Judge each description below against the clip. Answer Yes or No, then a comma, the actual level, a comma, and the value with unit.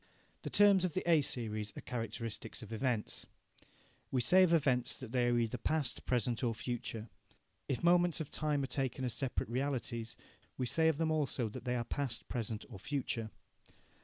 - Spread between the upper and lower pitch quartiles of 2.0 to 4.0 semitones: No, average, 4.4 semitones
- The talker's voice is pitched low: Yes, low, 125 Hz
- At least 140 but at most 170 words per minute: No, average, 185 wpm